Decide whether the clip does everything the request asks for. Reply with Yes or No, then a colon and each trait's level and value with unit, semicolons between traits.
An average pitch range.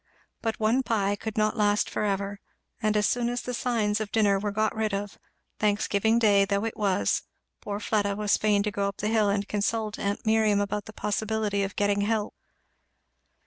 No: narrow, 1.4 semitones